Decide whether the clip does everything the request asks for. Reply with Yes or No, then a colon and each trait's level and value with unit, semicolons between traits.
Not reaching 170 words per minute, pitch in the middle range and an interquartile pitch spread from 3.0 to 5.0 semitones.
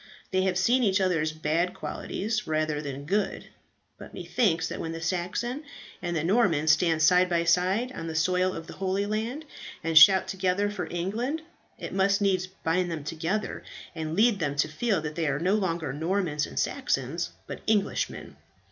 No: average, 180 wpm; medium, 180 Hz; average, 3.8 semitones